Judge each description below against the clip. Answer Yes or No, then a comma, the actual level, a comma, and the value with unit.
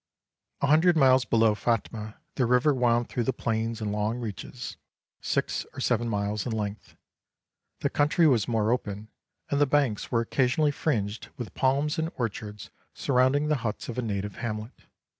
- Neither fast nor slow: Yes, average, 165 wpm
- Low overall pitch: Yes, low, 120 Hz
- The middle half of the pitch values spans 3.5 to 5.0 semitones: Yes, average, 3.8 semitones